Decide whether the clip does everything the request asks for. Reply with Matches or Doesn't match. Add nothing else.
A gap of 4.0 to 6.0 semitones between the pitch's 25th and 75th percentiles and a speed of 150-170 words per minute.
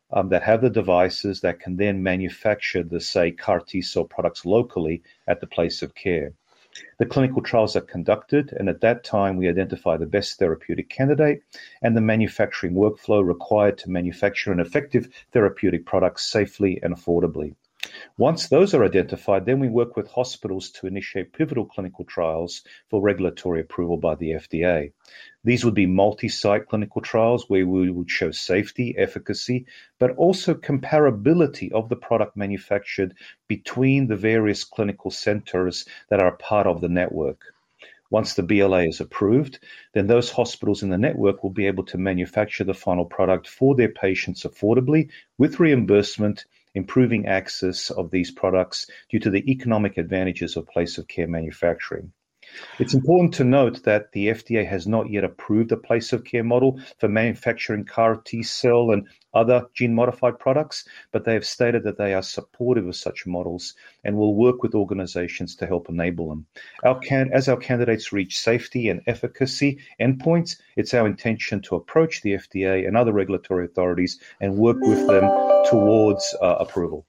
Matches